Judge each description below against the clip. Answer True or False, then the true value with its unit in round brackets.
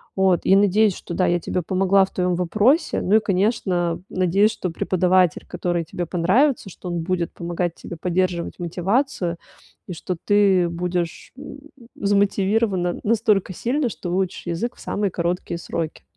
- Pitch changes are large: False (2.7 semitones)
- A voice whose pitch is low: False (185 Hz)